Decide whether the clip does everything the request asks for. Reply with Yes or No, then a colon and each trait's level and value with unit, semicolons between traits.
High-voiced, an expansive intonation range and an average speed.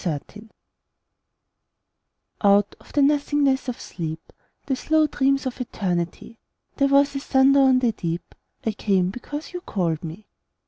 Yes: very high, 250 Hz; wide, 6.9 semitones; average, 150 wpm